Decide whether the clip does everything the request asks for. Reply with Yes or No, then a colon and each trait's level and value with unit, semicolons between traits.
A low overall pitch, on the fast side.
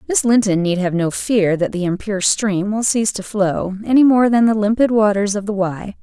No: high, 205 Hz; fast, 230 wpm